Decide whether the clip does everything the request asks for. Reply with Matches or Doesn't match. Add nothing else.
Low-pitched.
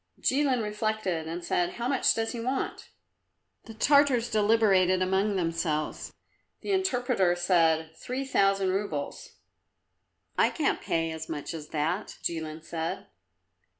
Doesn't match